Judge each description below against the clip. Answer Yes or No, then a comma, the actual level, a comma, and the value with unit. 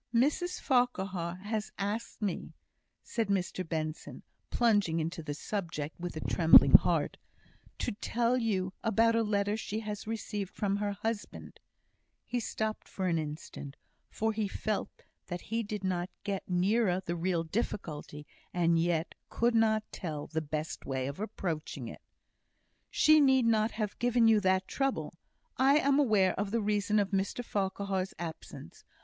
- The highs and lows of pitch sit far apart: No, average, 4.4 semitones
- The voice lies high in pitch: Yes, high, 200 Hz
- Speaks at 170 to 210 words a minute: No, average, 155 wpm